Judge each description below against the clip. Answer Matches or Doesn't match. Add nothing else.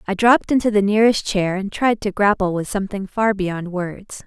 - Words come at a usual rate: Doesn't match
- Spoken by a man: Doesn't match